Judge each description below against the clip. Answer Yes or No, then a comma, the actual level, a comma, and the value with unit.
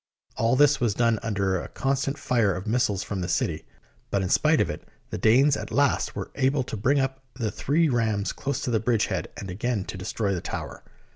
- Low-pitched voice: Yes, low, 115 Hz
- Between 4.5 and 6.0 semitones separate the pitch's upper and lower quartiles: Yes, average, 5.1 semitones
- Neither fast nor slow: No, fast, 220 wpm